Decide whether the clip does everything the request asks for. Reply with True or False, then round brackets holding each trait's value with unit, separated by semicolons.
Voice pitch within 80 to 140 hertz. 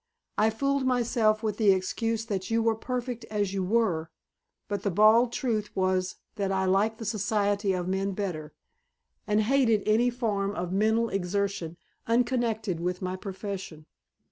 False (210 Hz)